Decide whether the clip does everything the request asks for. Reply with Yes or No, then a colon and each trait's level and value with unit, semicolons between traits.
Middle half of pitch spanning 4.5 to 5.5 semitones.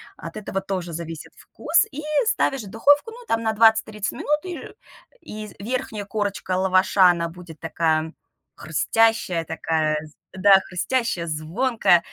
Yes: average, 5.1 semitones